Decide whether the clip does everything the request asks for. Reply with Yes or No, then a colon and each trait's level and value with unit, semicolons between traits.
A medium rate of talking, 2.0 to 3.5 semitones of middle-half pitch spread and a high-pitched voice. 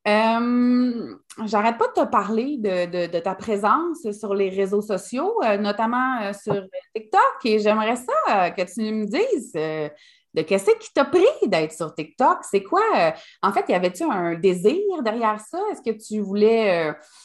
No: average, 185 wpm; wide, 5.6 semitones; high, 215 Hz